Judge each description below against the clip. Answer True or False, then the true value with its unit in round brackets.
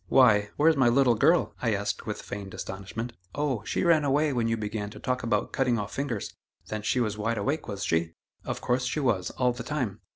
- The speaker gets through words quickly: True (220 wpm)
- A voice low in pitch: True (115 Hz)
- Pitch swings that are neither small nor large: True (4.4 semitones)